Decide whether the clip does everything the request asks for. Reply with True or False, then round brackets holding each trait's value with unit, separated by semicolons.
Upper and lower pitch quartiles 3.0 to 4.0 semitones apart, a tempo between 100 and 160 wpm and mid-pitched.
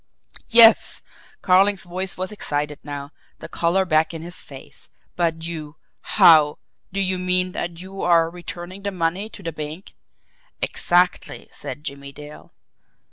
True (3.3 semitones; 140 wpm; 175 Hz)